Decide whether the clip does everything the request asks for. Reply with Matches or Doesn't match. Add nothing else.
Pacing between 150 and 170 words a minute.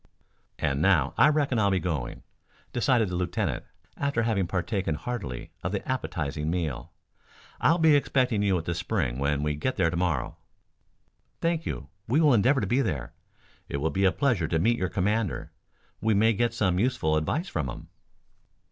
Doesn't match